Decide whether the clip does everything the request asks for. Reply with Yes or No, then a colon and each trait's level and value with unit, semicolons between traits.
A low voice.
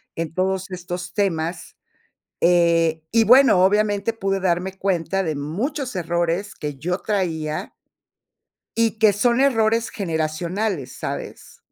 No: medium, 185 Hz